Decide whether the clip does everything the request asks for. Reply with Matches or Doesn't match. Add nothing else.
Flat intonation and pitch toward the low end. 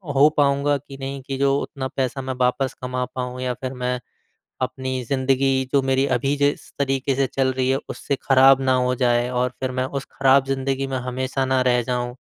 Matches